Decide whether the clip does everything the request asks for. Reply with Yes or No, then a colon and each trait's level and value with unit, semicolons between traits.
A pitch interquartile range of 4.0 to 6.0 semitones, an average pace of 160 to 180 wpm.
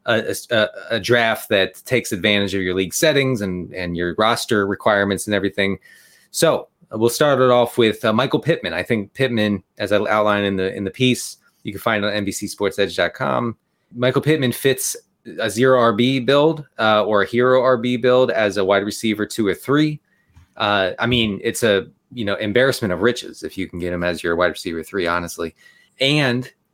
No: average, 4.3 semitones; average, 195 wpm